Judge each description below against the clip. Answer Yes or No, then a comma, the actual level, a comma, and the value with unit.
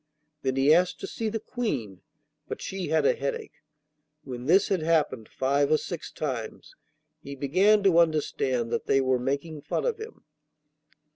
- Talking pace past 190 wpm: No, average, 165 wpm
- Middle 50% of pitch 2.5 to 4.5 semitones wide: No, wide, 5.6 semitones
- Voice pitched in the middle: Yes, medium, 150 Hz